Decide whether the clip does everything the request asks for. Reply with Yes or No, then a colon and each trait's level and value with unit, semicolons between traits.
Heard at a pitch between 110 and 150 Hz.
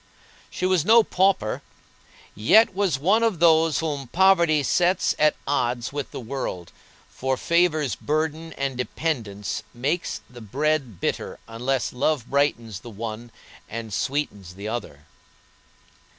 Yes: medium, 140 Hz